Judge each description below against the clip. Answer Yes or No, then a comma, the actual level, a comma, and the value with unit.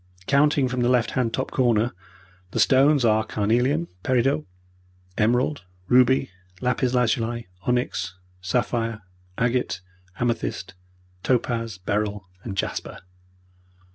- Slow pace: Yes, slow, 105 wpm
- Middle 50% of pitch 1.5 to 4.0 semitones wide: Yes, average, 2.7 semitones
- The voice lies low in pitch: Yes, low, 120 Hz